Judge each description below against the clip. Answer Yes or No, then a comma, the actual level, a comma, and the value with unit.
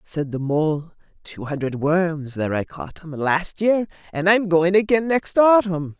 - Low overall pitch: No, medium, 170 Hz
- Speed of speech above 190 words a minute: No, average, 170 wpm